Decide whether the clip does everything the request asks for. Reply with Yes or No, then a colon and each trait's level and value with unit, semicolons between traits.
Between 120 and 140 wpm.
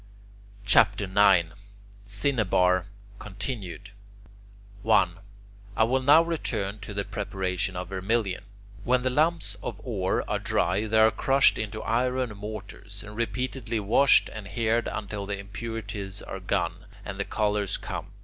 Yes: slow, 135 wpm